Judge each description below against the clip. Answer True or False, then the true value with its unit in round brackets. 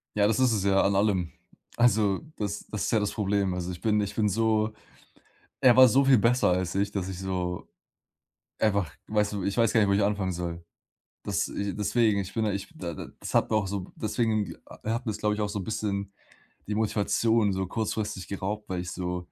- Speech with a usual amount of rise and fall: False (2.2 semitones)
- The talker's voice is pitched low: True (105 Hz)